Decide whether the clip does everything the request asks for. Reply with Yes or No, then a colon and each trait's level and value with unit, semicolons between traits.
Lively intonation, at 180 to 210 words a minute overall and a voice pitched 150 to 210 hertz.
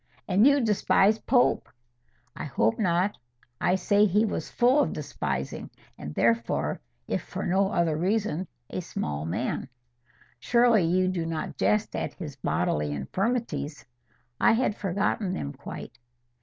No: wide, 7.4 semitones; average, 140 wpm; medium, 185 Hz